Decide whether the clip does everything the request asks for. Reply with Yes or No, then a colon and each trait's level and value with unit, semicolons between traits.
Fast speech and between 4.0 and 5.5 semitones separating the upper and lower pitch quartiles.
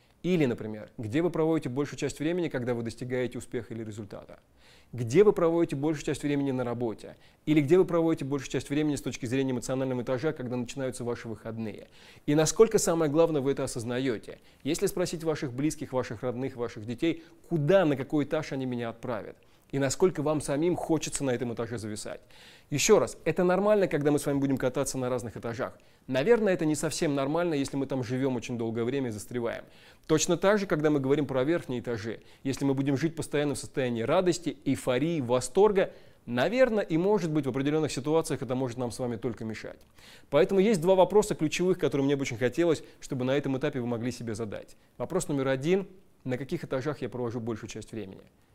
Yes: fast, 195 wpm; average, 4.5 semitones